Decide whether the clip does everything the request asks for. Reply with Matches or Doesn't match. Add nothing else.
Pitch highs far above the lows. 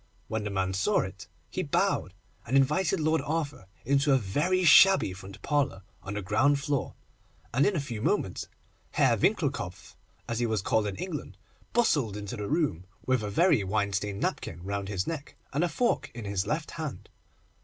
Matches